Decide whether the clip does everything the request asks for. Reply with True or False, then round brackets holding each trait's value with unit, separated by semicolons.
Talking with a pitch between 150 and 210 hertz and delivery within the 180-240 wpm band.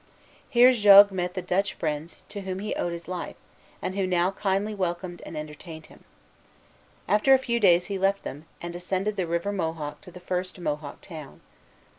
True (185 Hz; 185 wpm)